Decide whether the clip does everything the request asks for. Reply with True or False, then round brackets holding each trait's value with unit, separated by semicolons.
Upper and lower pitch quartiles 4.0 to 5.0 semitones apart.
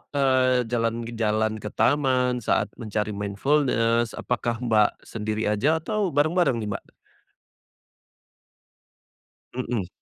False (3.5 semitones)